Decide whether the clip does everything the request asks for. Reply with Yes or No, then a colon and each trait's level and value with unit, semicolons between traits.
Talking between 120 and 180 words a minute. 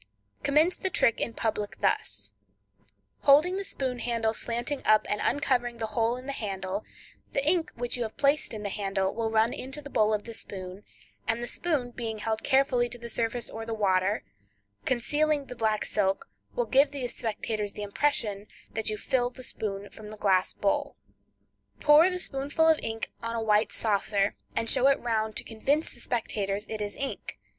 No: average, 190 wpm